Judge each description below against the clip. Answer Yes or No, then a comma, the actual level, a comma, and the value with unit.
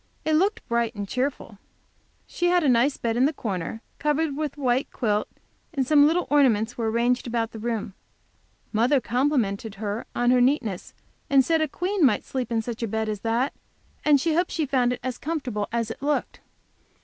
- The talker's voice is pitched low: No, very high, 250 Hz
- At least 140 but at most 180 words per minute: No, average, 195 wpm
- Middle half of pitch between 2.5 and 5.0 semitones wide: Yes, average, 4.4 semitones